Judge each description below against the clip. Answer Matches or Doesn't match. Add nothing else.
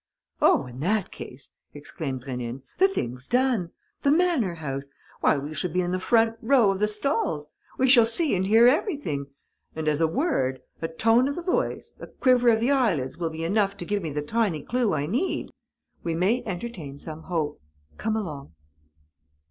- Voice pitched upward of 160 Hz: Matches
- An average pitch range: Doesn't match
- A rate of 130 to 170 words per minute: Doesn't match